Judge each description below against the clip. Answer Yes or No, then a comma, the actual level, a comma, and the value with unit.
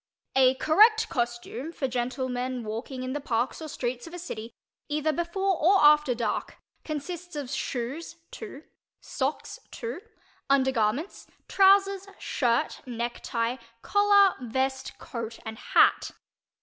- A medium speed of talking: No, slow, 125 wpm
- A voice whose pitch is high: Yes, very high, 270 Hz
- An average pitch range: No, wide, 6.0 semitones